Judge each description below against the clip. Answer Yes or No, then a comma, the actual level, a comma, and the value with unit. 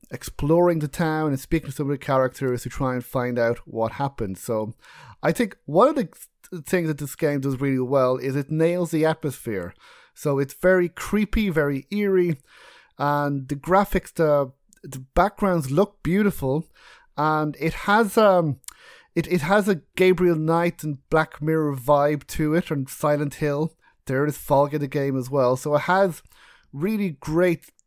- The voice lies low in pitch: No, medium, 150 Hz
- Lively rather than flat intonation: No, average, 4.2 semitones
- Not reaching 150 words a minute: No, average, 175 wpm